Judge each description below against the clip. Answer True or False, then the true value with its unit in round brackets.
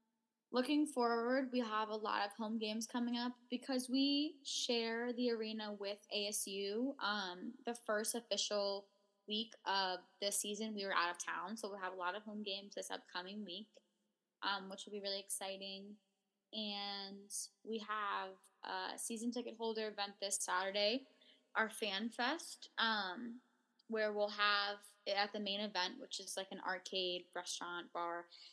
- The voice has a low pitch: False (210 Hz)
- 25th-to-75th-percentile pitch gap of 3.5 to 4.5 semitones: False (2.5 semitones)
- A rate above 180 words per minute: False (160 wpm)